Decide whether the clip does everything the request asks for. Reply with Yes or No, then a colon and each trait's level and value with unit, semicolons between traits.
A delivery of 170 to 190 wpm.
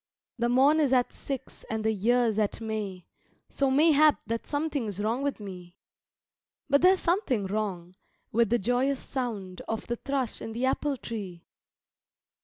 No: average, 160 wpm